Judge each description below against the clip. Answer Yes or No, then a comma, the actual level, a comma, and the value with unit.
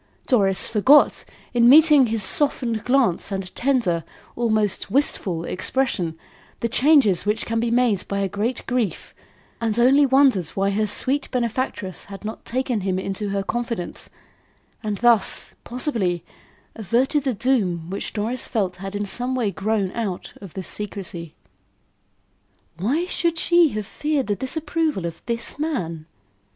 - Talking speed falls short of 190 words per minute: Yes, average, 145 wpm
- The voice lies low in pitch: No, high, 225 Hz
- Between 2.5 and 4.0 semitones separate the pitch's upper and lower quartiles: No, average, 4.9 semitones